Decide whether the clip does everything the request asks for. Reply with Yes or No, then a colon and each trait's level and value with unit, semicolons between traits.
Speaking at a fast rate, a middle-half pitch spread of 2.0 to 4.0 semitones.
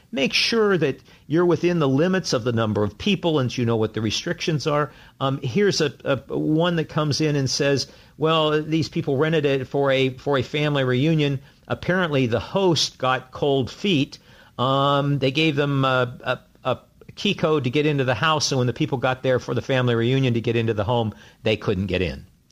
Yes: fast, 210 wpm; average, 3.7 semitones